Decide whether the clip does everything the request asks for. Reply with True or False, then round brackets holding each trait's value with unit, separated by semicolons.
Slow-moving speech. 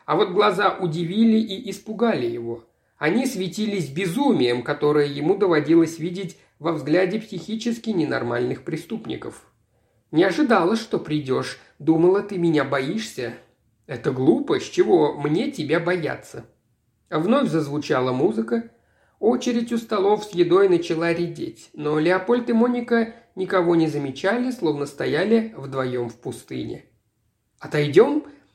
False (120 wpm)